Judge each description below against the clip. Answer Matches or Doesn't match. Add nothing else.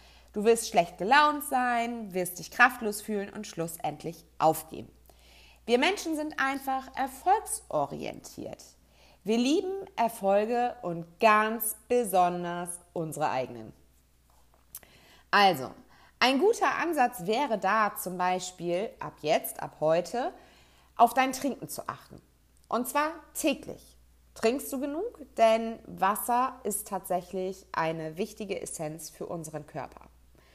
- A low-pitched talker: Doesn't match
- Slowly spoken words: Matches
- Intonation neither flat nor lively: Doesn't match